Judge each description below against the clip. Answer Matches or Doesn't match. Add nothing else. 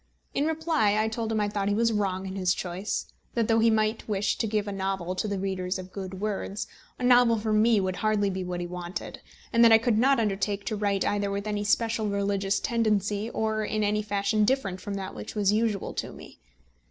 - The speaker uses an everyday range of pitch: Doesn't match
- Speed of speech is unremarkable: Doesn't match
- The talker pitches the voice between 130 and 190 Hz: Doesn't match